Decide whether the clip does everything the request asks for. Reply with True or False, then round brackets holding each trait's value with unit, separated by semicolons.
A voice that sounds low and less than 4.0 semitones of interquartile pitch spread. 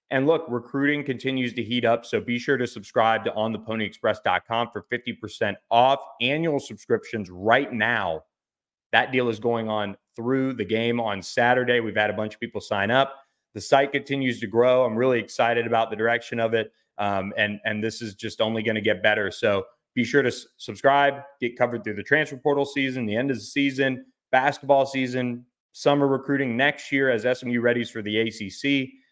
True (120 Hz; 3.2 semitones)